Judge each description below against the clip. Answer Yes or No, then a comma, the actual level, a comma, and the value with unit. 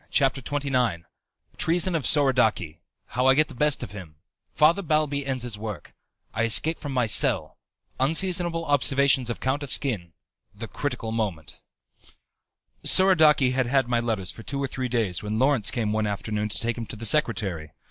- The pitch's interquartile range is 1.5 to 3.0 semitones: No, average, 4.9 semitones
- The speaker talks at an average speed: Yes, average, 170 wpm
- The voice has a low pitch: Yes, low, 125 Hz